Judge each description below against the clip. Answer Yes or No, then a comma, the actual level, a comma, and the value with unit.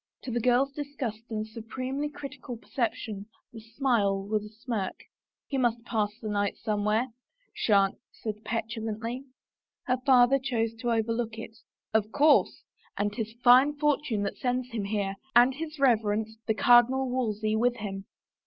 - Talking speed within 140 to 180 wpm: Yes, average, 160 wpm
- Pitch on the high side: Yes, high, 230 Hz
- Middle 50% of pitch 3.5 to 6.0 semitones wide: No, average, 3.1 semitones